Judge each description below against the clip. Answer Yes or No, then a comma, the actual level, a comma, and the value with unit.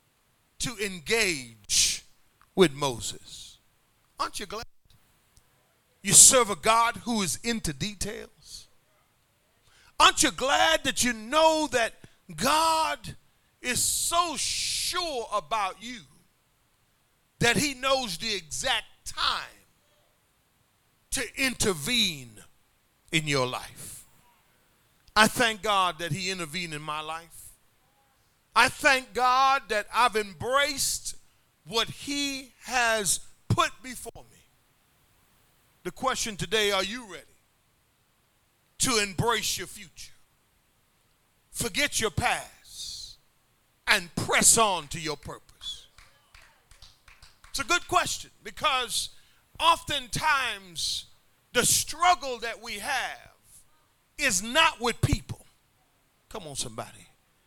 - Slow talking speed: Yes, slow, 100 wpm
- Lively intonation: Yes, wide, 8.1 semitones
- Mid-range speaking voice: No, high, 215 Hz